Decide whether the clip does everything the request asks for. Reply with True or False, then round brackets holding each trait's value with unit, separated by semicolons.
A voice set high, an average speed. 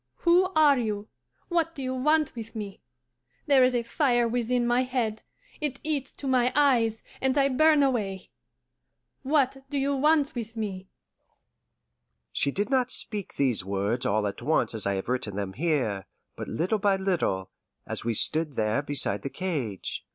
True (225 Hz; 170 wpm)